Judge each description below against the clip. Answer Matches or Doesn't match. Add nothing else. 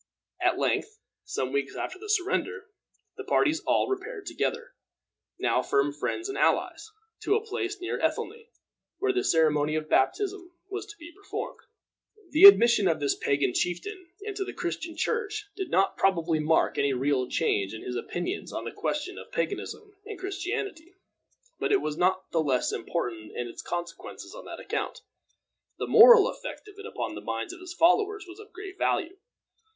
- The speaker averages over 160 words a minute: Matches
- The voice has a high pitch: Matches